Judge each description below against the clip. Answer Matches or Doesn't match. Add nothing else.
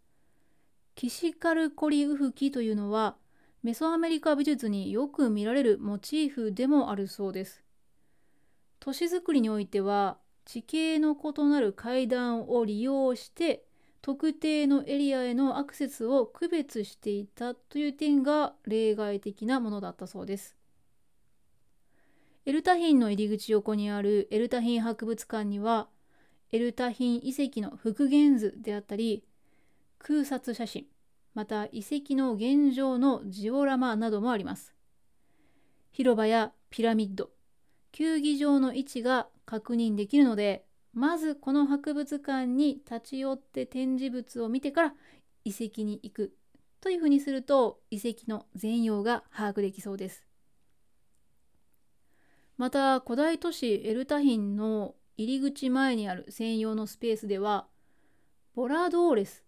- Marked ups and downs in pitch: Doesn't match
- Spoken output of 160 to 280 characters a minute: Matches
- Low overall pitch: Doesn't match